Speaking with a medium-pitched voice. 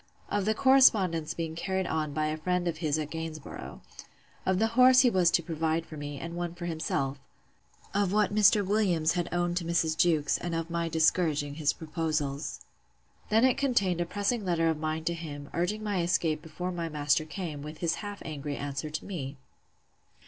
Yes: medium, 165 Hz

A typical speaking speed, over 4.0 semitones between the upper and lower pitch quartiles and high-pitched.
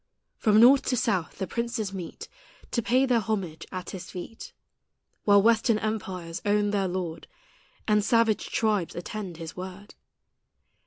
No: average, 145 wpm; average, 3.5 semitones; high, 205 Hz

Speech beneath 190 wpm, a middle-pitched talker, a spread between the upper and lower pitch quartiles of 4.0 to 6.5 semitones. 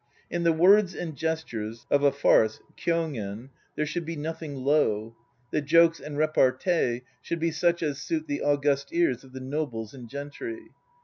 Yes: average, 170 wpm; medium, 150 Hz; average, 4.3 semitones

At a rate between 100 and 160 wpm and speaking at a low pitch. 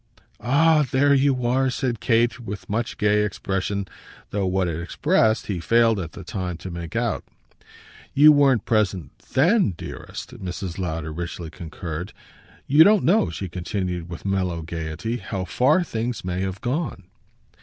Yes: average, 155 wpm; low, 100 Hz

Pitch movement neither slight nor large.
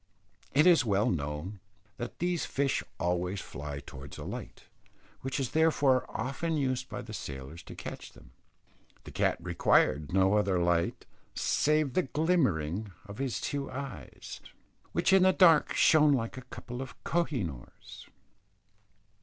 No: wide, 8.8 semitones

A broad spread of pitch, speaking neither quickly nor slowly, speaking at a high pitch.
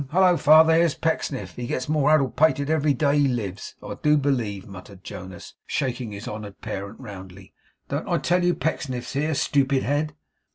No: wide, 6.4 semitones; average, 175 wpm; low, 135 Hz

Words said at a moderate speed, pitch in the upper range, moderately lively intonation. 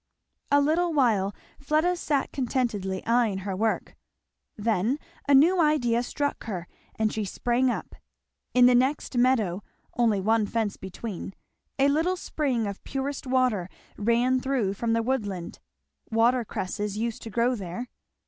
Yes: average, 145 wpm; high, 235 Hz; average, 4.2 semitones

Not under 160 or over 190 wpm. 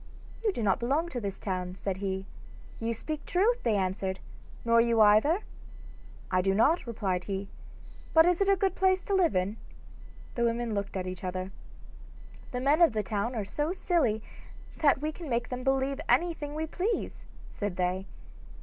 Yes: average, 180 wpm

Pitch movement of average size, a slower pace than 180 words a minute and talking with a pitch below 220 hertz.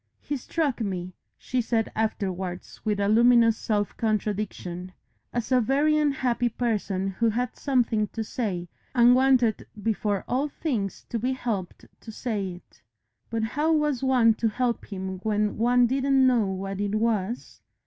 No: average, 3.6 semitones; average, 155 wpm; high, 225 Hz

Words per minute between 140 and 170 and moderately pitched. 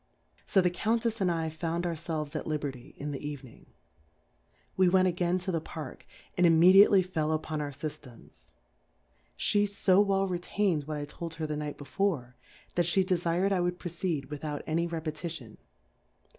Yes: average, 165 wpm; medium, 165 Hz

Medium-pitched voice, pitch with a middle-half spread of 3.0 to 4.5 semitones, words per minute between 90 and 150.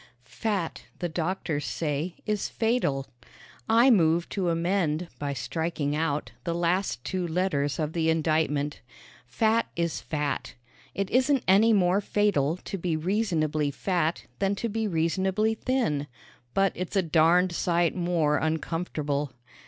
Yes: medium, 170 Hz; average, 4.0 semitones; slow, 135 wpm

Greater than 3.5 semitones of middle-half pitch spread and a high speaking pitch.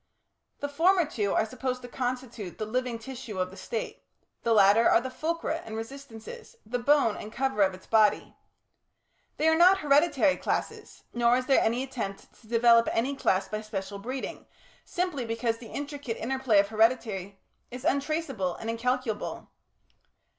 Yes: average, 4.0 semitones; high, 240 Hz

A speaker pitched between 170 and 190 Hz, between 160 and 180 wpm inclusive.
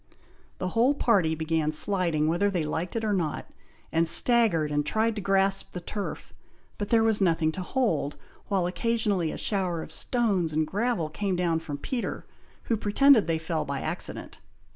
Yes: medium, 185 Hz; average, 175 wpm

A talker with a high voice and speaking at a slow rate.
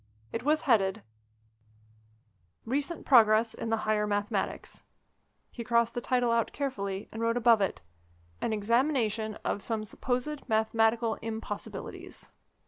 Yes: high, 225 Hz; slow, 125 wpm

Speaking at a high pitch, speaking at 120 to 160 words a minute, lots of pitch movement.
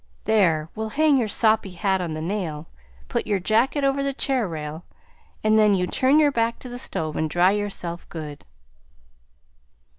No: high, 205 Hz; average, 175 wpm; wide, 6.3 semitones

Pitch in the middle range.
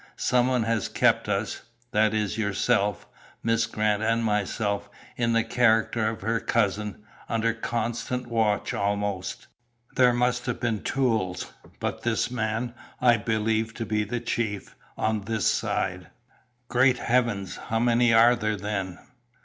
No: low, 110 Hz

